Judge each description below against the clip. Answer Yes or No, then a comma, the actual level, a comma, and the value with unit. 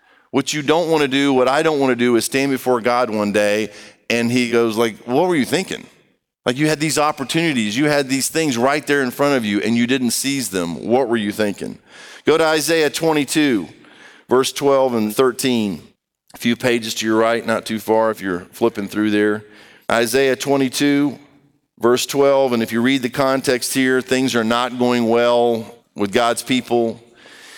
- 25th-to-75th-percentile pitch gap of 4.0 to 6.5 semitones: No, average, 3.4 semitones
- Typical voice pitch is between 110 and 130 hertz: Yes, low, 125 Hz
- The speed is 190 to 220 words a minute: Yes, average, 200 wpm